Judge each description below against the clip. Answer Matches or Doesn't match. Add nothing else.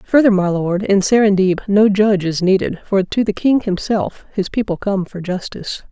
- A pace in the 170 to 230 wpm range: Matches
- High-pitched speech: Matches